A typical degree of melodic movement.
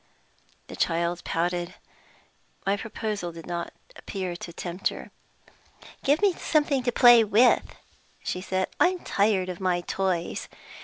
Yes: average, 4.7 semitones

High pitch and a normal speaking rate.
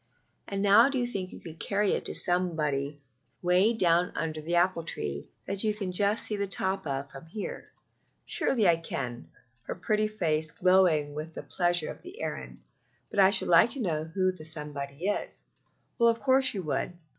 No: medium, 180 Hz; average, 190 wpm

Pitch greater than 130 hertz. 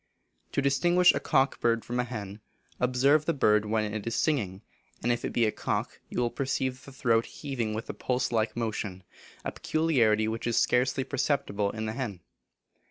No: low, 120 Hz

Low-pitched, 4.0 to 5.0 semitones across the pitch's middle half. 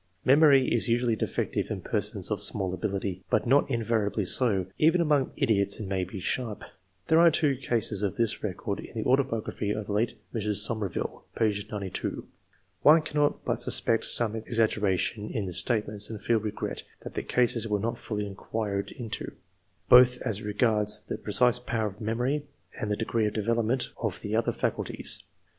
No: low, 110 Hz; average, 3.0 semitones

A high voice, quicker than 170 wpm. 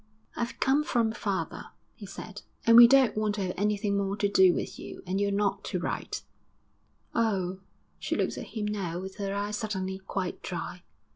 Yes: high, 200 Hz; average, 190 wpm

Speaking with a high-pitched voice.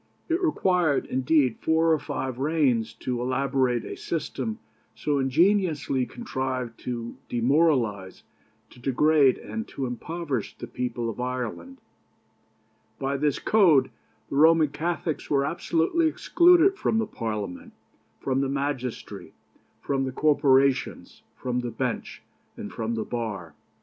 No: low, 135 Hz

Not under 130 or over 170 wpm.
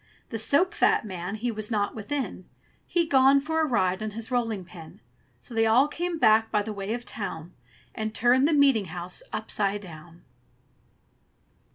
No: average, 180 wpm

